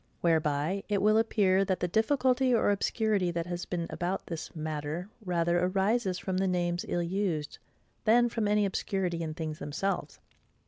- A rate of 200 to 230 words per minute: No, average, 165 wpm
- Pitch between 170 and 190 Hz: Yes, medium, 185 Hz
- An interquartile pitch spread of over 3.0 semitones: Yes, average, 3.4 semitones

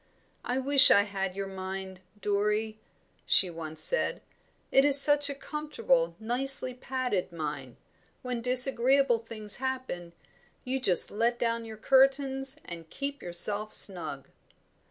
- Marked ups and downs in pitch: Yes, wide, 5.7 semitones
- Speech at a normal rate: No, slow, 130 wpm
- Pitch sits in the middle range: No, high, 230 Hz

